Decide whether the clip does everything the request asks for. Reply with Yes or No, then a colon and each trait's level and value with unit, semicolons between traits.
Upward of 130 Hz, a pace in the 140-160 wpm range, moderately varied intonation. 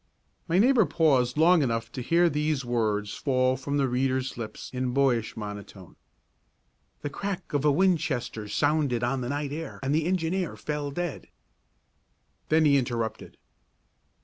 Yes: medium, 140 Hz; average, 150 wpm; average, 4.4 semitones